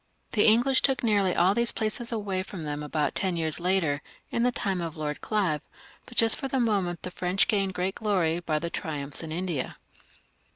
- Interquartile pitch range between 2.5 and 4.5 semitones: No, average, 4.9 semitones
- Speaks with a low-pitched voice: No, medium, 185 Hz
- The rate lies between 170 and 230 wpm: Yes, average, 200 wpm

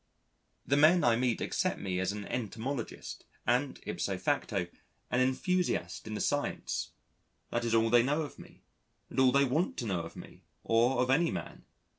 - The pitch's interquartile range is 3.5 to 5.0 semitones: Yes, average, 3.8 semitones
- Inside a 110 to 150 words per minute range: No, average, 180 wpm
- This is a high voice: No, low, 125 Hz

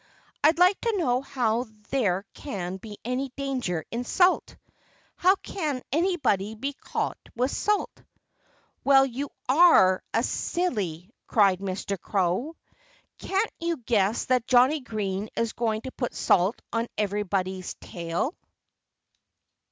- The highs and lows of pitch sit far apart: Yes, wide, 6.0 semitones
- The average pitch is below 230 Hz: No, high, 240 Hz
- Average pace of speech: No, slow, 125 wpm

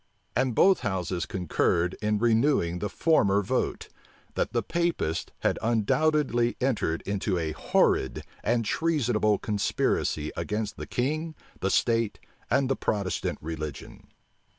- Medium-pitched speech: No, low, 110 Hz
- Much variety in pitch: Yes, wide, 5.9 semitones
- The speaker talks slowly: Yes, slow, 125 wpm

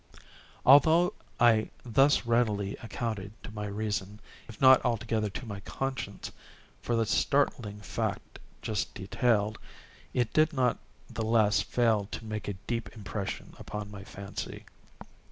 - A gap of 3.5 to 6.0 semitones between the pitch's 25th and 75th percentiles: No, average, 2.7 semitones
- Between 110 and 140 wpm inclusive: Yes, slow, 135 wpm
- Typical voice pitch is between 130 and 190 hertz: No, low, 110 Hz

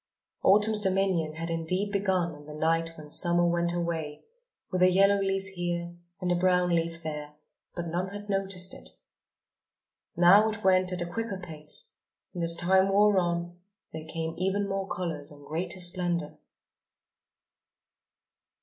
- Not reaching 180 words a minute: Yes, average, 150 wpm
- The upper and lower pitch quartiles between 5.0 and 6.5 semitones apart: No, narrow, 2.6 semitones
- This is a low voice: No, medium, 175 Hz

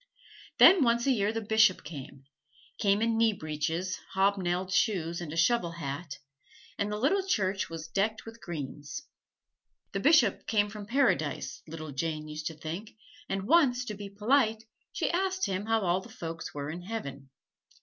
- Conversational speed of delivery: Yes, average, 165 wpm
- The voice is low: No, high, 195 Hz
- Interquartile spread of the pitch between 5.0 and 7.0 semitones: Yes, wide, 5.5 semitones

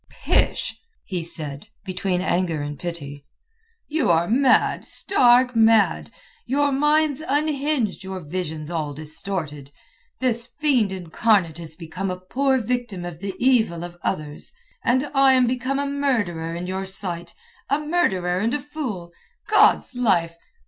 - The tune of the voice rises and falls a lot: Yes, wide, 7.3 semitones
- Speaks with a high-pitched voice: Yes, high, 195 Hz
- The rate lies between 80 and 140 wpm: Yes, slow, 135 wpm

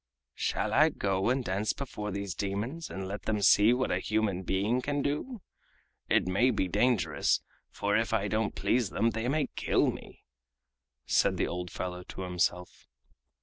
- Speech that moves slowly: No, average, 170 wpm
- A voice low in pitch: Yes, low, 105 Hz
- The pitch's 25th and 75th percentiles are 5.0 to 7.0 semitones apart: No, average, 4.5 semitones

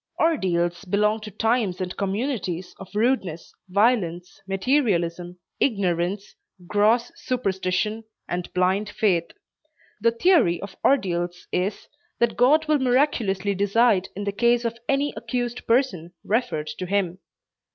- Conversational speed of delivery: No, slow, 120 wpm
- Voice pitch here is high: Yes, high, 200 Hz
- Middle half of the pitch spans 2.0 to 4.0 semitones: No, average, 4.8 semitones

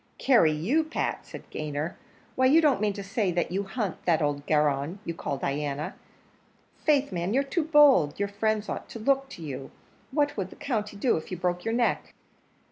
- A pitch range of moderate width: No, wide, 8.7 semitones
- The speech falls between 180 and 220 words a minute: Yes, average, 195 wpm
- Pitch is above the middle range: Yes, high, 200 Hz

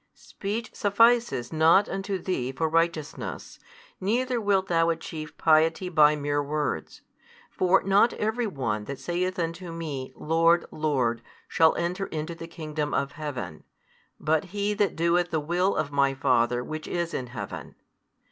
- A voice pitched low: No, medium, 165 Hz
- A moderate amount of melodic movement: Yes, average, 4.0 semitones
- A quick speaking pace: No, average, 145 wpm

